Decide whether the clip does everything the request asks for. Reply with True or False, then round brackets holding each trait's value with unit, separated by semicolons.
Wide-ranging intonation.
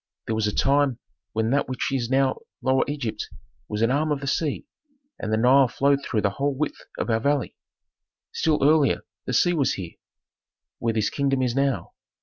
False (3.6 semitones)